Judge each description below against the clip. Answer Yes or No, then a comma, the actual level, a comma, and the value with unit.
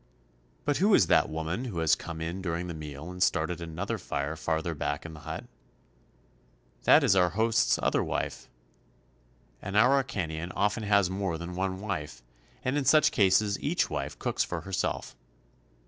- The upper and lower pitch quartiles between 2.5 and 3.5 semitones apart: No, average, 4.2 semitones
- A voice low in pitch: Yes, very low, 90 Hz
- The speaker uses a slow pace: No, average, 170 wpm